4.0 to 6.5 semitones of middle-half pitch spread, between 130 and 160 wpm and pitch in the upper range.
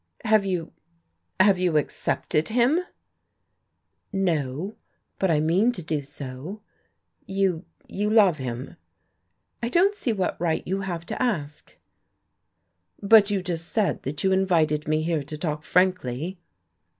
No: average, 4.4 semitones; slow, 135 wpm; medium, 180 Hz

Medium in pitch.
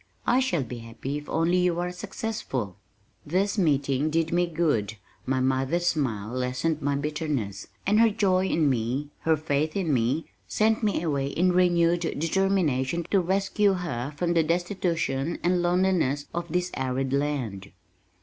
Yes: medium, 160 Hz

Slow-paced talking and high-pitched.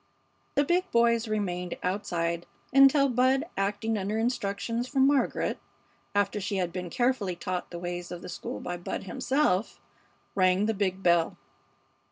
No: average, 150 wpm; high, 200 Hz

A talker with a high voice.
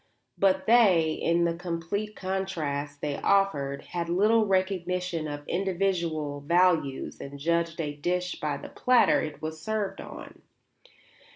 No: medium, 170 Hz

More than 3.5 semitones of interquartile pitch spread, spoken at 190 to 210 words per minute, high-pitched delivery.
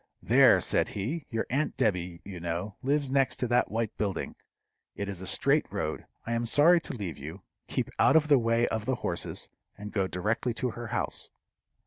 No: average, 4.8 semitones; average, 195 wpm; low, 115 Hz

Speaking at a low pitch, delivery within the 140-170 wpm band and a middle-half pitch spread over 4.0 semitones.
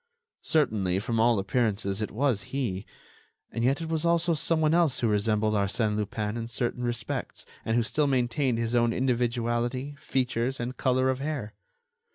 No: low, 120 Hz; average, 165 wpm; average, 3.5 semitones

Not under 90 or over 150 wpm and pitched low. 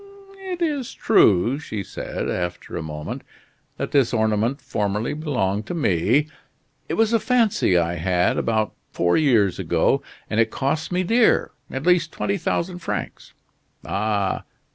Yes: average, 145 wpm; low, 120 Hz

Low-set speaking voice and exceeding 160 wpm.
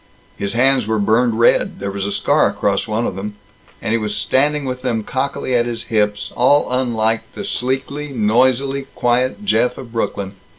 Yes: low, 120 Hz; average, 180 wpm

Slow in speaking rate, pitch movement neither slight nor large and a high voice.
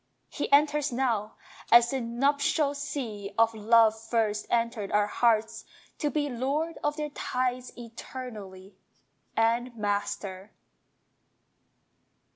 Yes: slow, 105 wpm; average, 4.3 semitones; high, 235 Hz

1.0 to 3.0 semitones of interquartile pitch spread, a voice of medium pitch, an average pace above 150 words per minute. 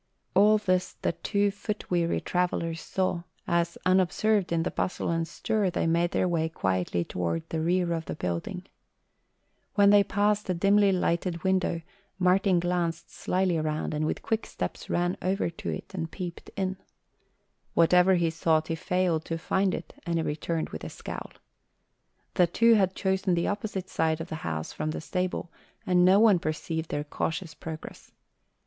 Yes: average, 2.7 semitones; medium, 175 Hz; average, 170 wpm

